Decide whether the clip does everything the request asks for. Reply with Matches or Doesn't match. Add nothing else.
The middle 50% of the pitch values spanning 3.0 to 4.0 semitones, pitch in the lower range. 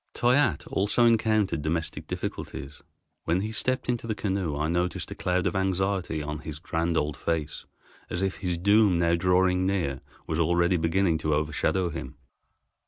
Matches